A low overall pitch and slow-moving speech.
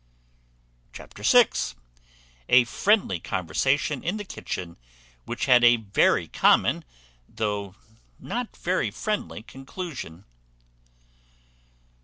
Yes: low, 125 Hz; slow, 90 wpm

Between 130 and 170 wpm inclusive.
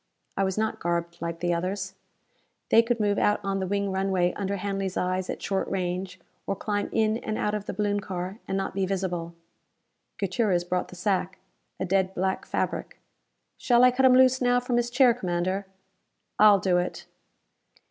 No: average, 185 wpm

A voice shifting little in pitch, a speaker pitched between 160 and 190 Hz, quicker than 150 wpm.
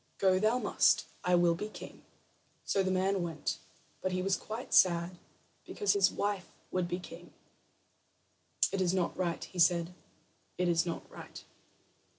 Yes: narrow, 1.9 semitones; medium, 185 Hz; average, 160 wpm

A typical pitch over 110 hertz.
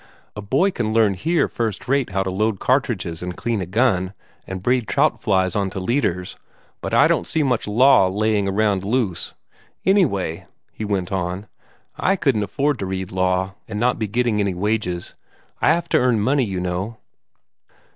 No: low, 105 Hz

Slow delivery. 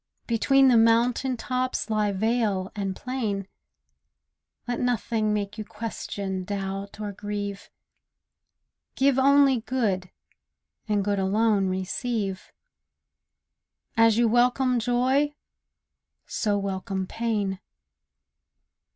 Yes: slow, 100 wpm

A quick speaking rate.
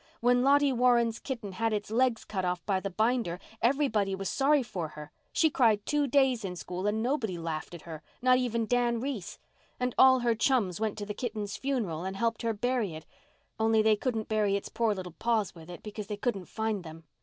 Yes: fast, 210 wpm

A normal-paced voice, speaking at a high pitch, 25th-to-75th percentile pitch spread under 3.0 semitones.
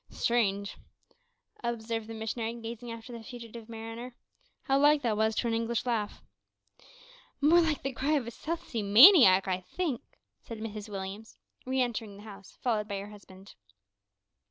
Yes: average, 160 wpm; high, 225 Hz; narrow, 2.6 semitones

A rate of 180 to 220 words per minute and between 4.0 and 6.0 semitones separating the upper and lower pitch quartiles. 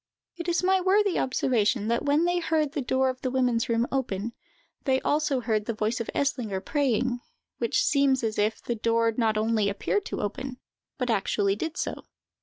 Yes: average, 190 wpm; average, 4.3 semitones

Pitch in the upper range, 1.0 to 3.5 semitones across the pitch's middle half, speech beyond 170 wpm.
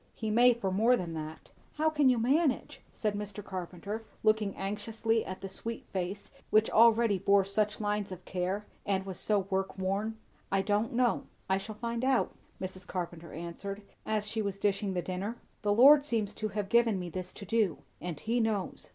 Yes: high, 205 Hz; average, 3.0 semitones; average, 190 wpm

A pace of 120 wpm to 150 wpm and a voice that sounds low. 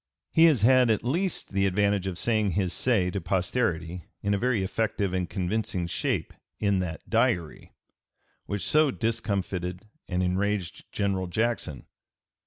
Yes: average, 145 wpm; low, 100 Hz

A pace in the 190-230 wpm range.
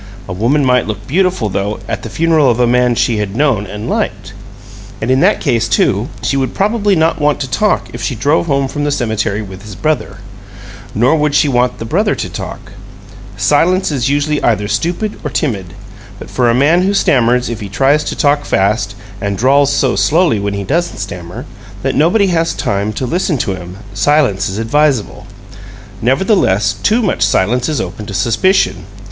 Yes: average, 195 wpm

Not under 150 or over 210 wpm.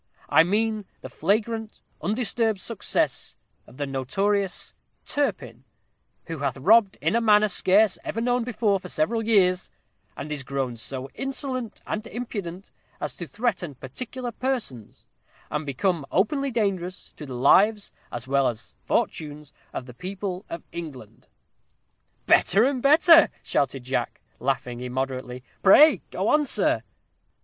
No: slow, 135 wpm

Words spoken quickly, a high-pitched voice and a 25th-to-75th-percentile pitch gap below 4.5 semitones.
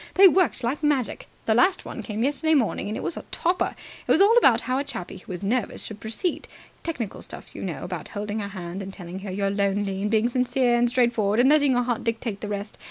No: fast, 240 wpm; high, 225 Hz; average, 4.8 semitones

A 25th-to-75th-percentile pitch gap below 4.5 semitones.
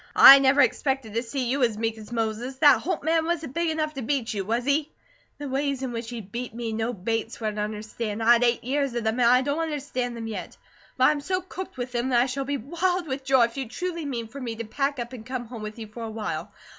Yes: average, 3.8 semitones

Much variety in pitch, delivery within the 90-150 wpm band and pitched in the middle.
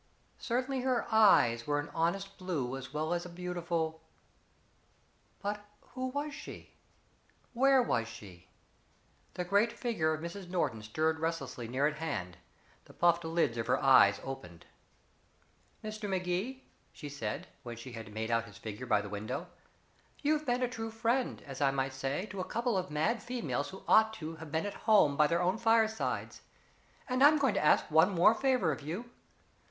No: wide, 8.2 semitones; average, 175 wpm; medium, 170 Hz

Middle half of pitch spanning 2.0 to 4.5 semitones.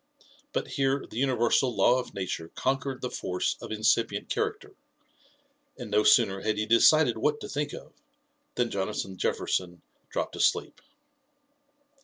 No: average, 5.1 semitones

